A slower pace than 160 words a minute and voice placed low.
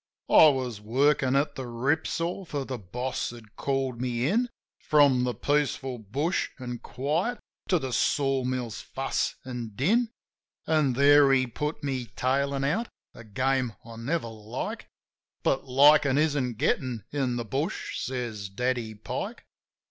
Yes: average, 150 wpm; low, 130 Hz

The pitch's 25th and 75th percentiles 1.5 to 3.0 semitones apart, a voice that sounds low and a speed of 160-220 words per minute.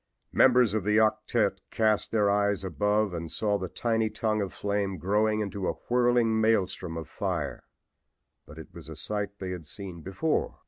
Yes: narrow, 2.5 semitones; low, 105 Hz; average, 175 wpm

